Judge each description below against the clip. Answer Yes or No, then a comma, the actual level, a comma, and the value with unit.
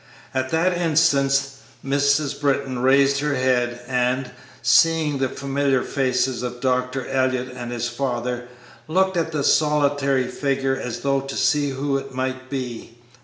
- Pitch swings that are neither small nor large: No, narrow, 1.9 semitones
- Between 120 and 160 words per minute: Yes, average, 145 wpm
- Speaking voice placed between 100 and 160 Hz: Yes, low, 135 Hz